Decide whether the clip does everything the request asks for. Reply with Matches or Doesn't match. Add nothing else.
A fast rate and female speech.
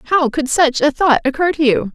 Matches